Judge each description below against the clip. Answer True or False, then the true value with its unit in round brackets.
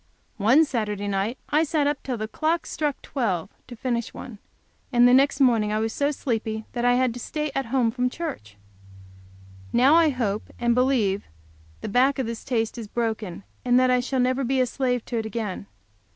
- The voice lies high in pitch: True (245 Hz)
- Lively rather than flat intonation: False (3.4 semitones)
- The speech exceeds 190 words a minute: True (200 wpm)